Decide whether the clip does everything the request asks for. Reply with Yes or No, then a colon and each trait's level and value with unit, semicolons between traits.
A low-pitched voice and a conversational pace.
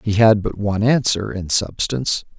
Yes: low, 105 Hz; average, 175 wpm